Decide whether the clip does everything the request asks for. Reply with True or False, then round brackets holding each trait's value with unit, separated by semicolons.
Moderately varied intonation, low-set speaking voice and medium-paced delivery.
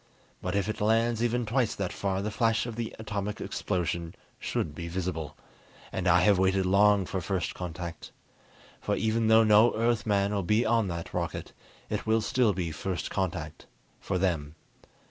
True (3.7 semitones; 100 Hz; 170 wpm)